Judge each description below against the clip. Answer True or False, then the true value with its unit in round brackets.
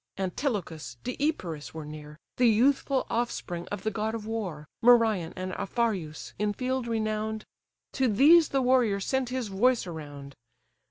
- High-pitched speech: True (215 Hz)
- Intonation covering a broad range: True (5.9 semitones)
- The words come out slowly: False (145 wpm)